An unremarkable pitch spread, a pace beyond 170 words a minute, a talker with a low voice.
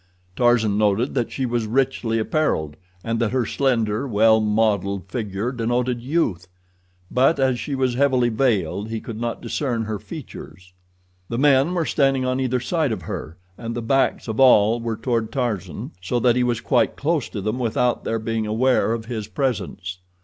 Yes: average, 3.1 semitones; average, 180 wpm; low, 115 Hz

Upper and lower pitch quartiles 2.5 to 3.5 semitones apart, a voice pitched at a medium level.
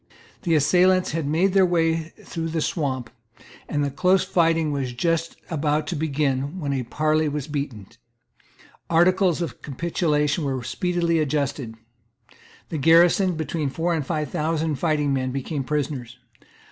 Yes: average, 2.9 semitones; medium, 155 Hz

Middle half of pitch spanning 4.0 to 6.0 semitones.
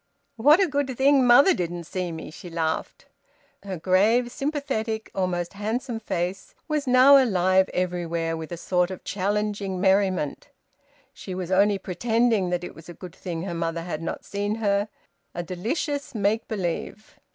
Yes: average, 4.6 semitones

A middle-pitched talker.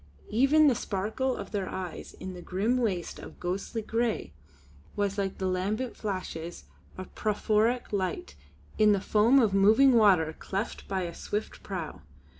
No: high, 205 Hz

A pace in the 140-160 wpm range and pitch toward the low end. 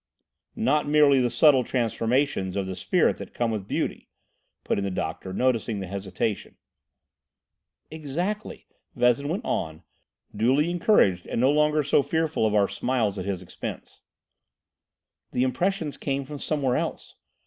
Yes: average, 145 wpm; low, 125 Hz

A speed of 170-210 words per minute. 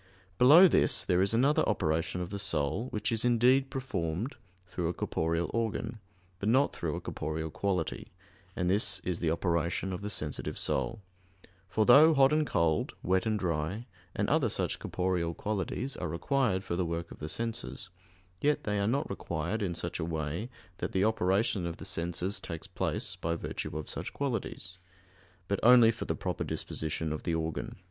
Yes: average, 185 wpm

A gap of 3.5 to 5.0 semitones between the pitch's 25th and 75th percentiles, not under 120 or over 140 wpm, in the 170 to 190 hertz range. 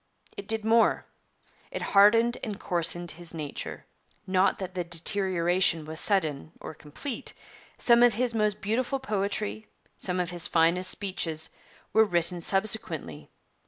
Yes: average, 4.3 semitones; slow, 135 wpm; medium, 185 Hz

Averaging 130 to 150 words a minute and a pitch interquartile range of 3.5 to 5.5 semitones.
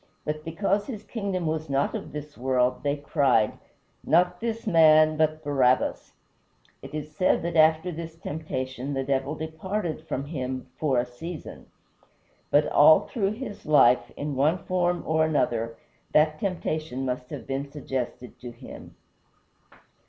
Yes: average, 145 wpm; average, 3.8 semitones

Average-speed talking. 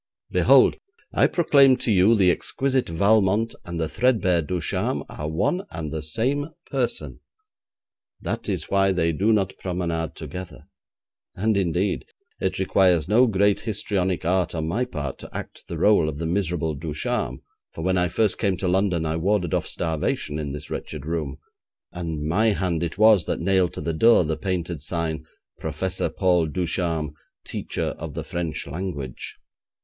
Yes: average, 165 wpm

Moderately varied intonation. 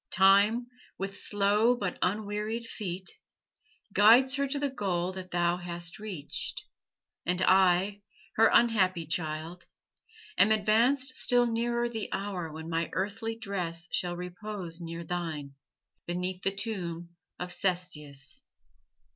Yes: average, 3.8 semitones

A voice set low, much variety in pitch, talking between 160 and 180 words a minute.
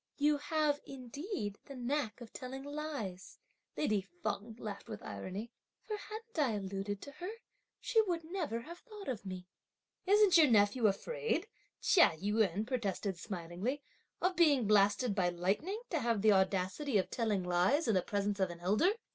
No: high, 230 Hz; wide, 7.3 semitones; average, 165 wpm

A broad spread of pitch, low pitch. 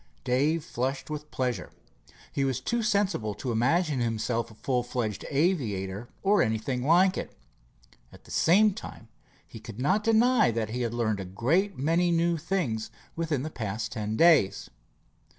Yes: wide, 7.1 semitones; low, 130 Hz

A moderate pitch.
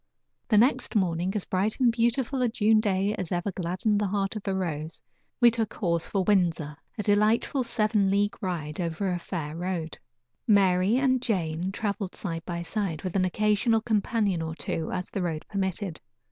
No: high, 195 Hz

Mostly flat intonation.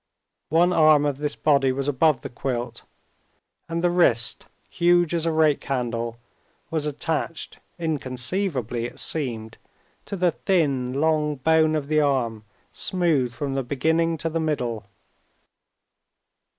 No: average, 4.2 semitones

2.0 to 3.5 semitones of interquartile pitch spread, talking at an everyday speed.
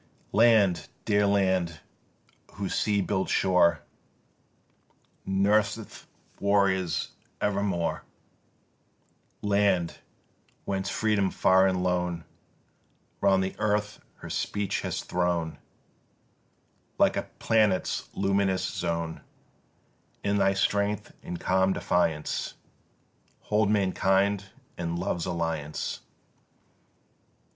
No: narrow, 2.4 semitones; slow, 85 wpm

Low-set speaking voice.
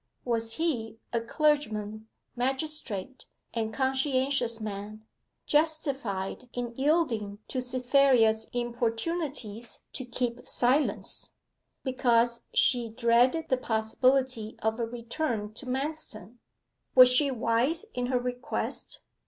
No: high, 245 Hz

